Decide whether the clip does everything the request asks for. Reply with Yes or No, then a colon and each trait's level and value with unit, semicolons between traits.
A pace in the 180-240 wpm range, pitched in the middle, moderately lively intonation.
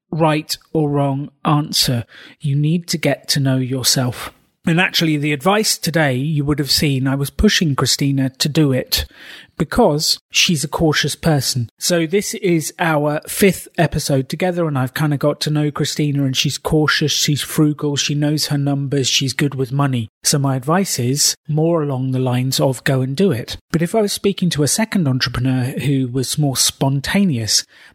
Yes: average, 185 wpm; medium, 150 Hz; average, 3.5 semitones